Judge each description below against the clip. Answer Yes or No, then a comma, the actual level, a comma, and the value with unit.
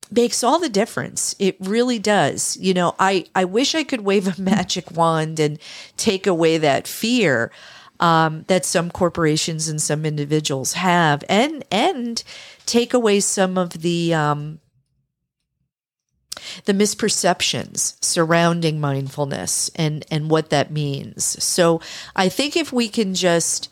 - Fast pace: No, average, 140 wpm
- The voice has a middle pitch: Yes, medium, 175 Hz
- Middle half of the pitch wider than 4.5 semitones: Yes, average, 4.9 semitones